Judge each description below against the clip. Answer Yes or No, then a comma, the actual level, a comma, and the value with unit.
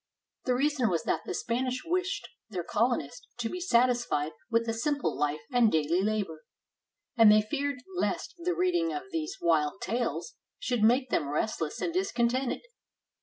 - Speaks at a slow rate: No, average, 165 wpm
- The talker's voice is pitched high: Yes, high, 240 Hz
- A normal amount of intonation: No, wide, 6.5 semitones